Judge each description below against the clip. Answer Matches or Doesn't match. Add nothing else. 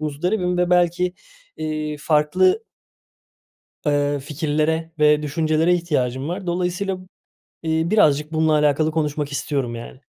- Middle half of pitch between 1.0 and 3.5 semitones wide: Matches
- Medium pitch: Matches